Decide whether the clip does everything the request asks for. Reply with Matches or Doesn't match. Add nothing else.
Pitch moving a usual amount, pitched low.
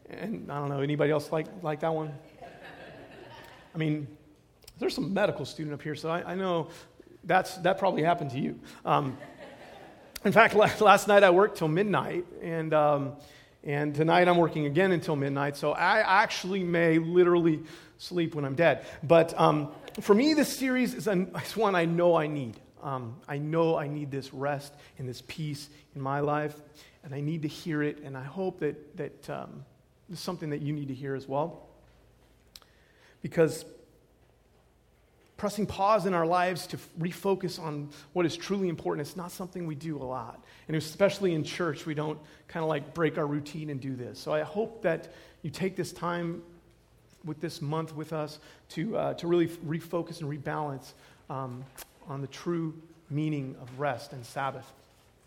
Doesn't match